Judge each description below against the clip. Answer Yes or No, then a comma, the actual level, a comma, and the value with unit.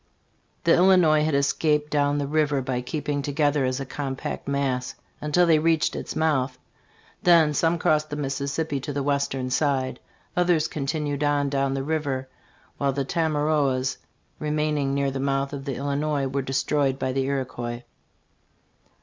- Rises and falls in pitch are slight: Yes, narrow, 2.0 semitones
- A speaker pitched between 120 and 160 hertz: Yes, medium, 140 Hz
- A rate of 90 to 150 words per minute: No, average, 160 wpm